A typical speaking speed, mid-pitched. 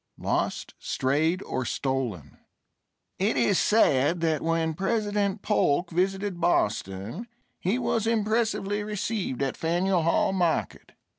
No: slow, 115 wpm; medium, 180 Hz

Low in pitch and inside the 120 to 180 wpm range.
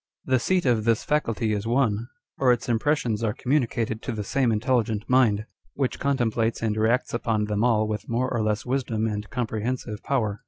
No: low, 115 Hz; average, 190 wpm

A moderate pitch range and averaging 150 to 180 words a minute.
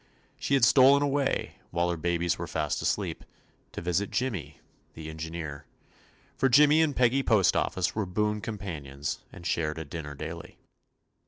No: wide, 7.3 semitones; average, 170 wpm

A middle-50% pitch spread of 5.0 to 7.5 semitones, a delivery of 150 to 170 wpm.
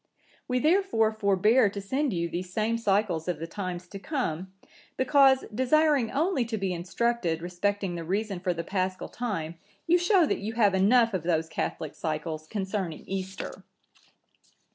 Yes: average, 5.3 semitones; average, 160 wpm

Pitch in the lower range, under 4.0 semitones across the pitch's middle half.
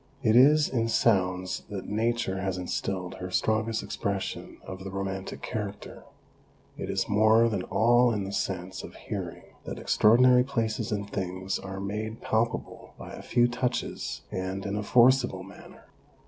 Yes: low, 105 Hz; average, 3.4 semitones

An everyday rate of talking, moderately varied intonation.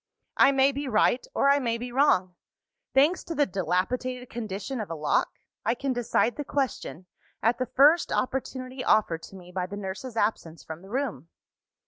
No: average, 180 wpm; wide, 5.9 semitones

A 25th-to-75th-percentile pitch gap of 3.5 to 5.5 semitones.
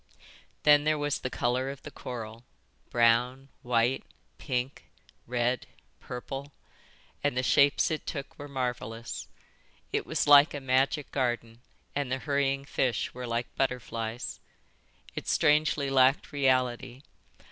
No: narrow, 2.5 semitones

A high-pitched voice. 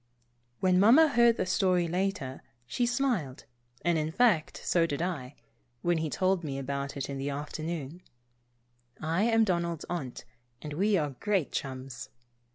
No: medium, 170 Hz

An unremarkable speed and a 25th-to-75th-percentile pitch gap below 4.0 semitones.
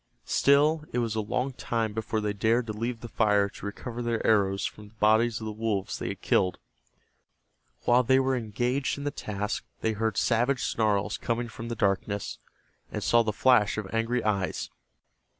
Yes: average, 185 wpm; narrow, 2.5 semitones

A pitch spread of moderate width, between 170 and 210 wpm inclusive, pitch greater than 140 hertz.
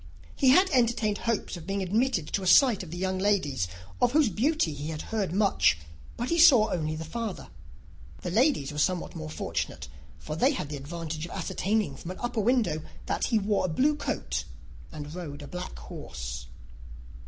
No: wide, 7.1 semitones; average, 190 wpm; medium, 185 Hz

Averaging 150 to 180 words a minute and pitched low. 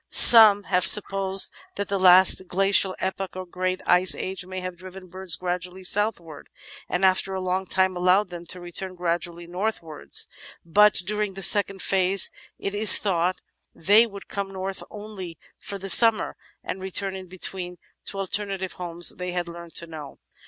No: average, 170 wpm; medium, 185 Hz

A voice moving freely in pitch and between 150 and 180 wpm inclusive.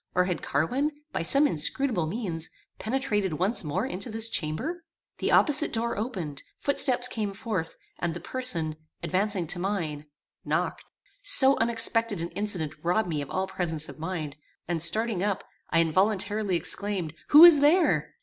Yes: wide, 5.9 semitones; average, 155 wpm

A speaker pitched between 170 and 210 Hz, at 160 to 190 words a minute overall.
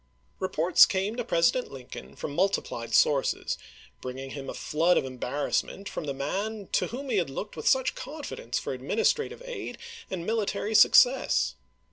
Yes: high, 190 Hz; average, 165 wpm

